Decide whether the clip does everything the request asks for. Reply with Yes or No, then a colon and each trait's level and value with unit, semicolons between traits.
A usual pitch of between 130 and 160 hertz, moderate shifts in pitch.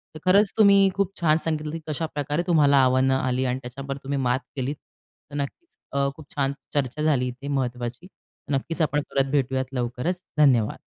Yes: medium, 140 Hz; average, 3.2 semitones